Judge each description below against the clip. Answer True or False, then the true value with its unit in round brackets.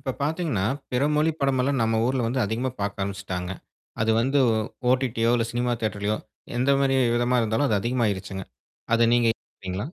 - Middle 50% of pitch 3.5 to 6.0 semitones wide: True (4.0 semitones)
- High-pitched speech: False (120 Hz)